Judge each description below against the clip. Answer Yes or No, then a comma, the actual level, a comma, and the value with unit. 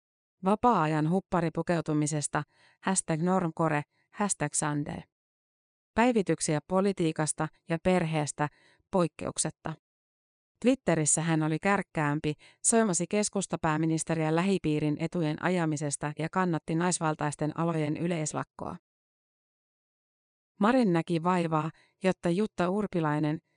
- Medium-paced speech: No, slow, 80 wpm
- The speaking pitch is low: No, medium, 165 Hz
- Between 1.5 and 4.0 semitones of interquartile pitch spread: Yes, average, 3.3 semitones